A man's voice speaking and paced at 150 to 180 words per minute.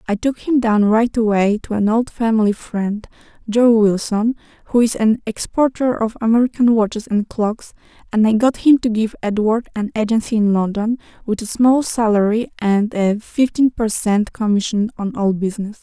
No: female; average, 175 wpm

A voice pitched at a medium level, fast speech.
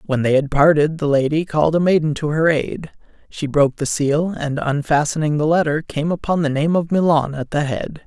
Yes: medium, 150 Hz; fast, 215 wpm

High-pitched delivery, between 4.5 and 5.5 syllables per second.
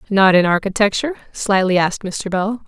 No: high, 200 Hz; 5.7 syllables/s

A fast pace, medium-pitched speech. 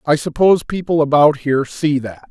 No: average, 180 wpm; medium, 150 Hz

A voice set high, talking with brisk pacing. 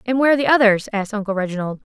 Yes: high, 220 Hz; fast, 250 wpm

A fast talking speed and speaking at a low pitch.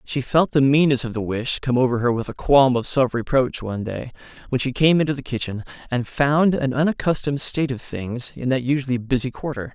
Yes: fast, 220 wpm; low, 130 Hz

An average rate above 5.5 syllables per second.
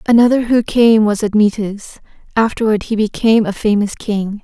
No: 5.1 syllables/s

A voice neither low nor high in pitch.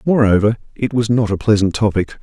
No: low, 110 Hz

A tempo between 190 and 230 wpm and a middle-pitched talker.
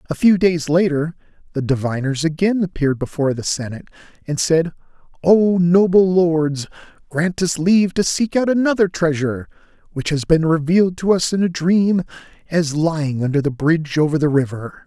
No: average, 165 wpm; medium, 165 Hz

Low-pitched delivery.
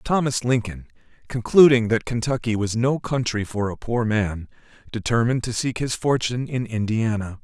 Yes: low, 115 Hz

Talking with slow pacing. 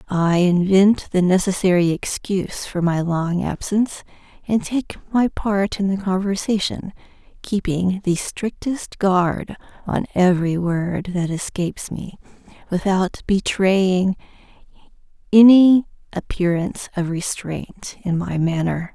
Yes: slow, 110 wpm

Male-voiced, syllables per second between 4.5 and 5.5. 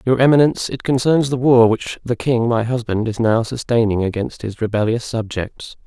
Yes: male; 5.1 syllables/s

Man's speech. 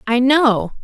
No: female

